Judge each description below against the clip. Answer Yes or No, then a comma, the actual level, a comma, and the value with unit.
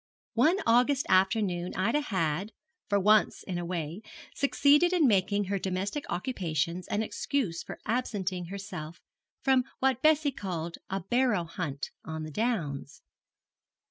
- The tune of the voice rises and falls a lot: Yes, wide, 6.0 semitones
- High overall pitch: Yes, high, 200 Hz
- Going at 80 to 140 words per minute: Yes, slow, 135 wpm